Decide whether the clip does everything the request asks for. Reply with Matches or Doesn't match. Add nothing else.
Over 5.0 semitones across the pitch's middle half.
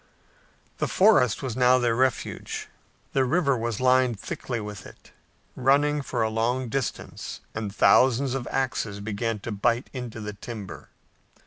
Doesn't match